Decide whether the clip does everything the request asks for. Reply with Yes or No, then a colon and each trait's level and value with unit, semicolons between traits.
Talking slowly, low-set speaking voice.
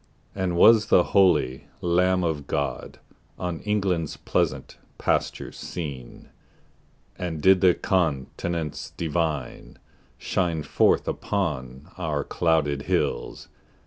Yes: slow, 100 wpm; very low, 85 Hz